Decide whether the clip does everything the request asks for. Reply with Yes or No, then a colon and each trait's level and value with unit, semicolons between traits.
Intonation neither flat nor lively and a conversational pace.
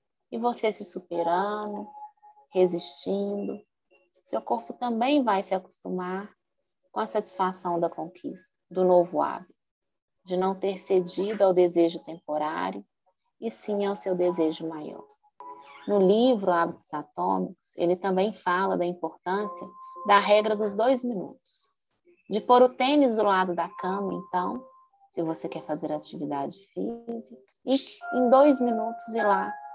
Yes: average, 4.9 semitones; average, 135 wpm